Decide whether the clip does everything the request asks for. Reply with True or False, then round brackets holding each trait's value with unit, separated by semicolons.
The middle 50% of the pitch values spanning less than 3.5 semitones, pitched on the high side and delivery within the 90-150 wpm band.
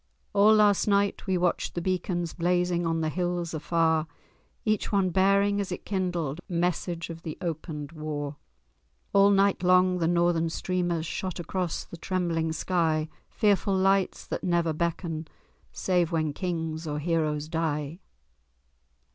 False (2.5 semitones; 175 Hz; 140 wpm)